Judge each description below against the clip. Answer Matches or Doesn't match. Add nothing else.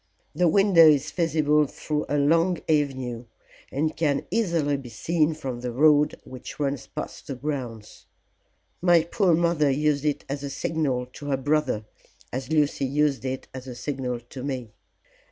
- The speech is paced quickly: Doesn't match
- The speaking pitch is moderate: Matches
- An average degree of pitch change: Matches